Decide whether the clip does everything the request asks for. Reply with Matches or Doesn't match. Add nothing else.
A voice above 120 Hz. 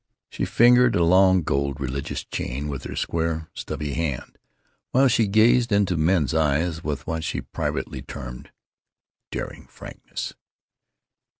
Doesn't match